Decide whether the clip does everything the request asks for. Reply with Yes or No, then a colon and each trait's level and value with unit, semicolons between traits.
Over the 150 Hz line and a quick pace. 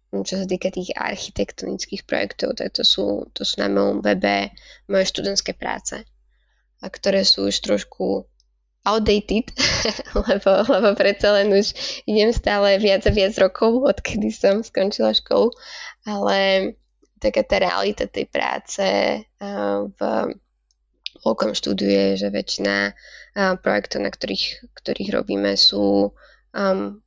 No: high, 190 Hz; average, 125 wpm